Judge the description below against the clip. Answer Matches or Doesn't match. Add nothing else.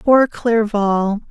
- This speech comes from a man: Doesn't match